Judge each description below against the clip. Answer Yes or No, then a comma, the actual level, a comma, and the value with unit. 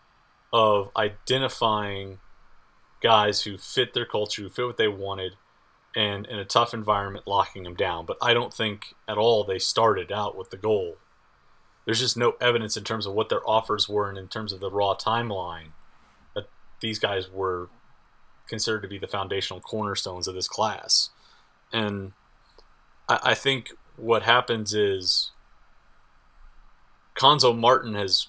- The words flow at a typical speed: Yes, average, 155 wpm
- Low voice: Yes, low, 105 Hz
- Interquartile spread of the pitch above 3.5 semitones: No, average, 3.1 semitones